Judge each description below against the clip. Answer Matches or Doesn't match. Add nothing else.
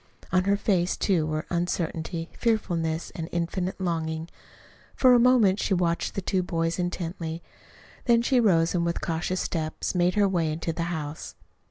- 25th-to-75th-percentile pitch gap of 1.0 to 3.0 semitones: Matches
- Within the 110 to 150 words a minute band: Doesn't match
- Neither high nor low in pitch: Matches